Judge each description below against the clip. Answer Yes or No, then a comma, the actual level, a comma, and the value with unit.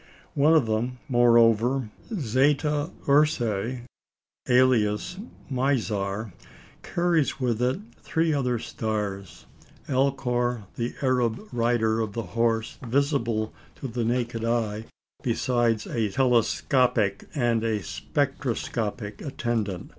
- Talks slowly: Yes, slow, 100 wpm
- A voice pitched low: Yes, low, 120 Hz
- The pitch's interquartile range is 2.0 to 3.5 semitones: Yes, average, 3.0 semitones